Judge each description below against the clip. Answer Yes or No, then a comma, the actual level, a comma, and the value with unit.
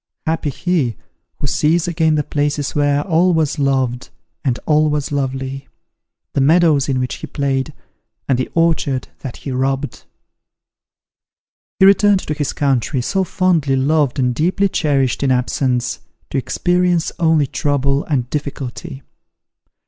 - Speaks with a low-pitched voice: No, medium, 145 Hz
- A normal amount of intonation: Yes, average, 3.2 semitones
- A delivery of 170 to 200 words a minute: No, average, 140 wpm